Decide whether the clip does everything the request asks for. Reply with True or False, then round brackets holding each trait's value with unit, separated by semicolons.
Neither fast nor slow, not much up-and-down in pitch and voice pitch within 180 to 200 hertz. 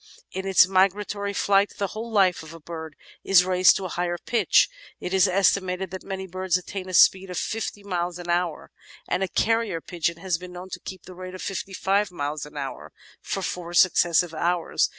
False (210 wpm; 1.9 semitones; 185 Hz)